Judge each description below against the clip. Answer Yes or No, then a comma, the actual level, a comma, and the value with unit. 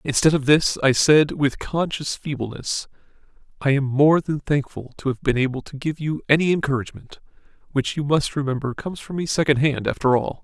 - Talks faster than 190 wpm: No, average, 180 wpm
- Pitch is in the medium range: Yes, medium, 145 Hz